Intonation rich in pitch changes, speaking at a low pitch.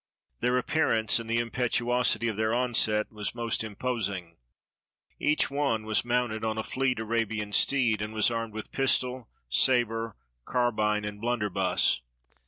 No: narrow, 2.4 semitones; low, 115 Hz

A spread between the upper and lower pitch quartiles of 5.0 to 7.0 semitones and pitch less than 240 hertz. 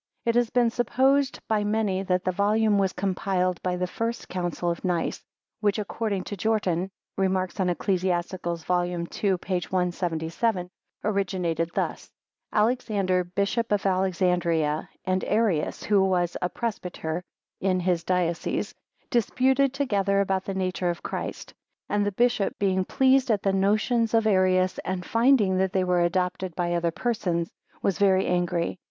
No: average, 2.9 semitones; high, 190 Hz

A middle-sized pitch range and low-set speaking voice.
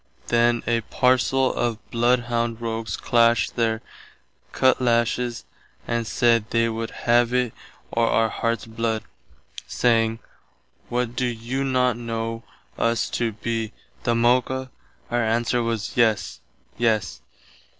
No: narrow, 1.0 semitones; low, 115 Hz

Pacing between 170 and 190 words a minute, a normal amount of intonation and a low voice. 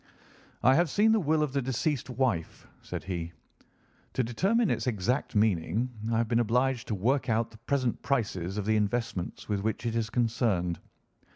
Yes: average, 180 wpm; average, 4.1 semitones; low, 115 Hz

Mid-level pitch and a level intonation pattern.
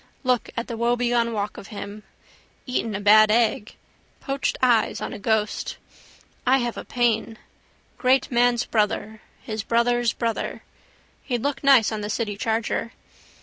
No: high, 230 Hz; narrow, 2.0 semitones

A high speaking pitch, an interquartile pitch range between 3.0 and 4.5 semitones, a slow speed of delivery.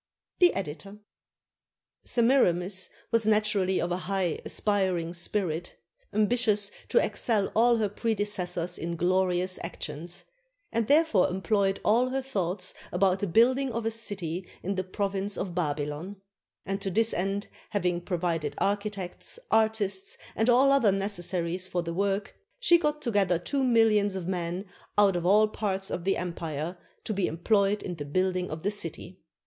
No: high, 195 Hz; average, 3.3 semitones; average, 155 wpm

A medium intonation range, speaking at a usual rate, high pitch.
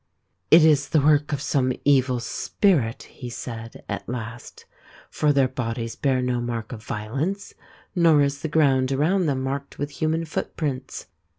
No: average, 3.7 semitones; average, 170 wpm; low, 135 Hz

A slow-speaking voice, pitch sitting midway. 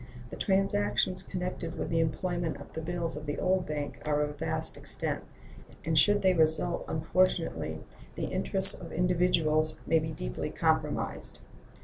No: average, 150 wpm; medium, 165 Hz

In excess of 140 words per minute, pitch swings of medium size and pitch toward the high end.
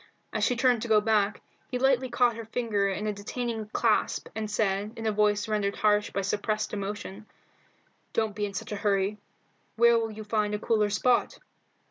No: average, 190 wpm; narrow, 1.7 semitones; high, 215 Hz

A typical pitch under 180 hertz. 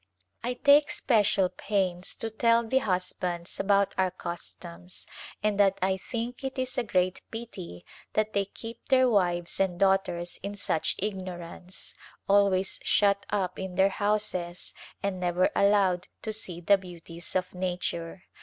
No: high, 190 Hz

